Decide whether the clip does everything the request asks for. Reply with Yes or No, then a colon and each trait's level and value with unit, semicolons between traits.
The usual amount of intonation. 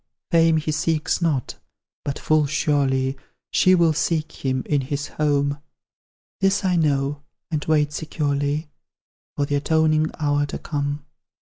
No: narrow, 1.8 semitones